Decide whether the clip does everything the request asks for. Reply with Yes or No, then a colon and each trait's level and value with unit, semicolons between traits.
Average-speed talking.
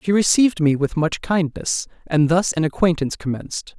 Yes: average, 175 wpm